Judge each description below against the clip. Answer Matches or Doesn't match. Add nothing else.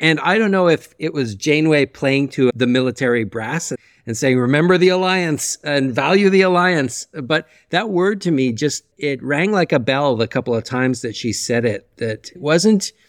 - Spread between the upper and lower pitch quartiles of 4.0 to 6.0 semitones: Matches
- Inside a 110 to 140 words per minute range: Doesn't match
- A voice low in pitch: Doesn't match